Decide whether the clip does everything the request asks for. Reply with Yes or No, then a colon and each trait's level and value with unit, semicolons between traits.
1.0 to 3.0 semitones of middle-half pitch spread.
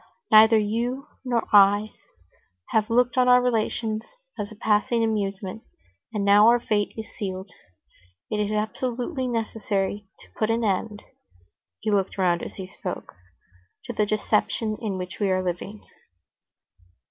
Yes: narrow, 2.6 semitones